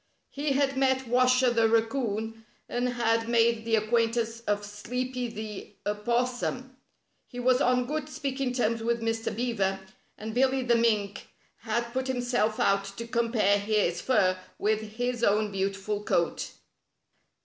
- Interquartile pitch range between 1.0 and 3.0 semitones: Yes, average, 2.7 semitones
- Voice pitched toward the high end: Yes, high, 230 Hz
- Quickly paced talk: No, average, 145 wpm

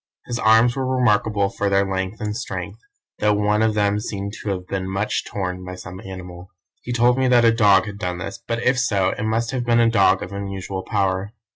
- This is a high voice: No, low, 105 Hz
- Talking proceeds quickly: Yes, fast, 225 wpm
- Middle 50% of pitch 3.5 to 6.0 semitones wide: No, average, 3.1 semitones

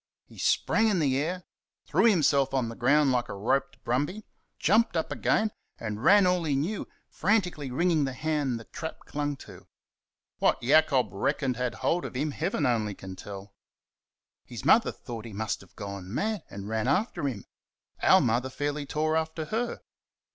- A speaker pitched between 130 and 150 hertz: Yes, medium, 140 Hz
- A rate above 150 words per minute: Yes, average, 175 wpm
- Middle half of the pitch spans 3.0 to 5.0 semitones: No, wide, 5.6 semitones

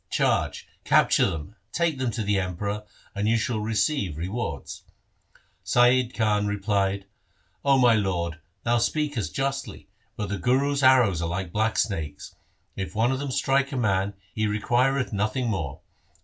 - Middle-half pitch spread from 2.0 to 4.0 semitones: No, average, 4.7 semitones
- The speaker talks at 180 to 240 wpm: No, average, 160 wpm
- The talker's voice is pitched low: Yes, low, 110 Hz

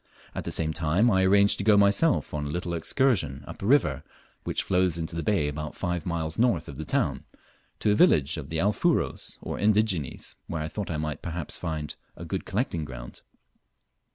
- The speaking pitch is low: Yes, very low, 85 Hz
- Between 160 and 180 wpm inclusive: No, average, 200 wpm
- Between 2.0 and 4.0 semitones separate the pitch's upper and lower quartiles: No, average, 4.6 semitones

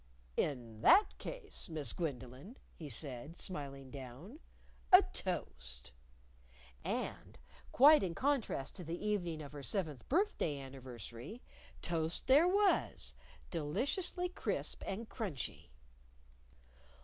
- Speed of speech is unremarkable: No, slow, 105 wpm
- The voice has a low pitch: No, medium, 165 Hz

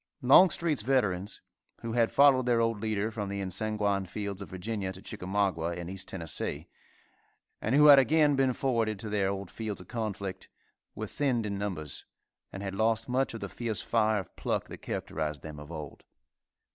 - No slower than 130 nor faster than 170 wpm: No, average, 180 wpm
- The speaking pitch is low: Yes, low, 105 Hz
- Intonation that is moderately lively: Yes, average, 3.6 semitones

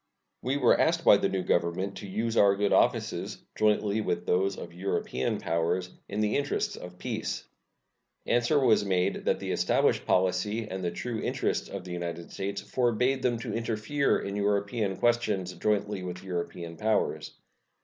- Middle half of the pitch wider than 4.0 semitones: No, average, 3.6 semitones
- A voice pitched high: No, low, 100 Hz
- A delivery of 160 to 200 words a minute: Yes, average, 165 wpm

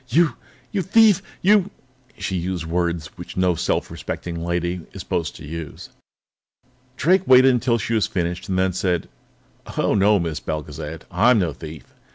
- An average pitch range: No, wide, 6.6 semitones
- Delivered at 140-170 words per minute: Yes, average, 165 wpm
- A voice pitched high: No, very low, 90 Hz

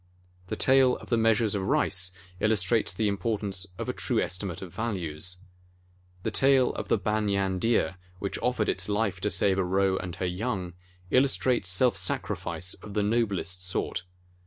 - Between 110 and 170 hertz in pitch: No, low, 100 Hz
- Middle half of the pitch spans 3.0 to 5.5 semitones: Yes, average, 3.5 semitones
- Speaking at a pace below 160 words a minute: No, average, 170 wpm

